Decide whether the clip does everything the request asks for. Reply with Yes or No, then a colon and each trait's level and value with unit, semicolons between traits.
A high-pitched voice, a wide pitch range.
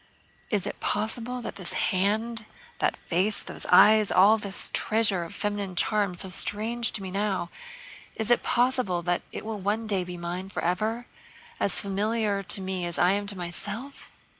No: high, 205 Hz; average, 3.0 semitones